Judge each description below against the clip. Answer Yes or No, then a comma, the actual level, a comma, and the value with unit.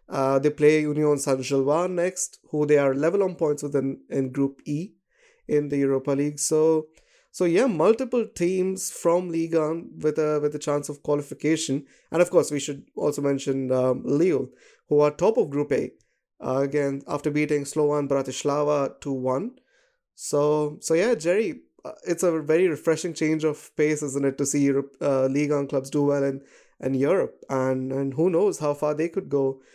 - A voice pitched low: No, medium, 150 Hz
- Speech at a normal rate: Yes, average, 185 wpm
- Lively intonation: No, narrow, 2.6 semitones